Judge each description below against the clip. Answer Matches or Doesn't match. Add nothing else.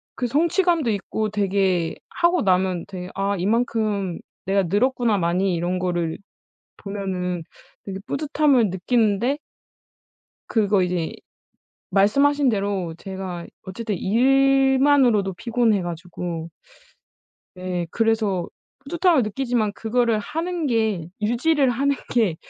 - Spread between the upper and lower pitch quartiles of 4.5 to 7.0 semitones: Matches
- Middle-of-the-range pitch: Doesn't match